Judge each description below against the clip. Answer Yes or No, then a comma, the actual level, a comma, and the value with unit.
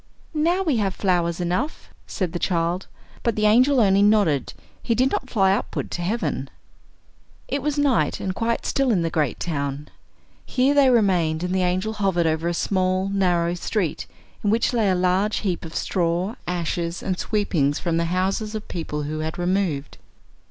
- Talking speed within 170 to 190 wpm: Yes, average, 180 wpm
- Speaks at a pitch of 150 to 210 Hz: Yes, medium, 185 Hz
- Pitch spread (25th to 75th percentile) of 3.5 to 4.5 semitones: Yes, average, 4.2 semitones